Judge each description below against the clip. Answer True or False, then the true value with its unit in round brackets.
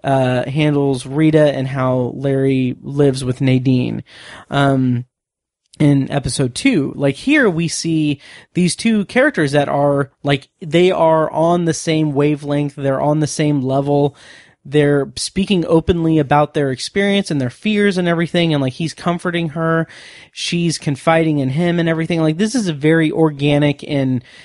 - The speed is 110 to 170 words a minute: True (150 wpm)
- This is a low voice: False (150 Hz)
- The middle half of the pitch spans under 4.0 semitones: True (3.3 semitones)